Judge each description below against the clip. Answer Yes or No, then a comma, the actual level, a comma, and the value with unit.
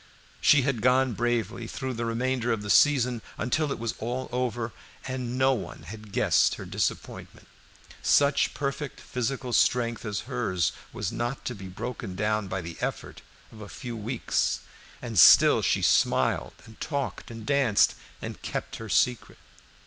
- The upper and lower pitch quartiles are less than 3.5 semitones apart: Yes, average, 2.9 semitones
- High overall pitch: No, low, 120 Hz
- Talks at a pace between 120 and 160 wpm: Yes, average, 155 wpm